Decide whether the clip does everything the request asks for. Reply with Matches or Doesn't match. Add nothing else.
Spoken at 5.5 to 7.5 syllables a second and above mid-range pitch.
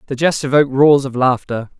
Doesn't match